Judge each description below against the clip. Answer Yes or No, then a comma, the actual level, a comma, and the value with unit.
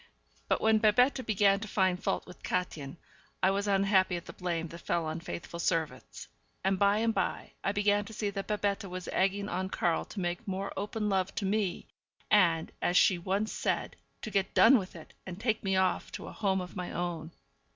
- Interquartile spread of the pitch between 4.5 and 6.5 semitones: No, narrow, 2.6 semitones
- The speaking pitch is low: No, high, 195 Hz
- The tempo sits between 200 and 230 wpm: Yes, fast, 205 wpm